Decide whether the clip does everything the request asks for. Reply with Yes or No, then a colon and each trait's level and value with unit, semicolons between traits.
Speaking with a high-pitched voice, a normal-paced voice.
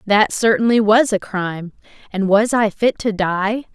Yes: high, 210 Hz; average, 175 wpm